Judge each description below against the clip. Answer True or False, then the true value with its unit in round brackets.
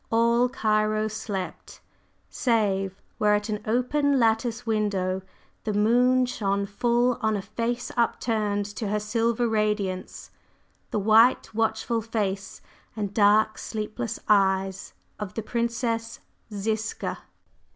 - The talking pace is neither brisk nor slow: False (120 wpm)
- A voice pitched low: False (215 Hz)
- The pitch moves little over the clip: True (2.1 semitones)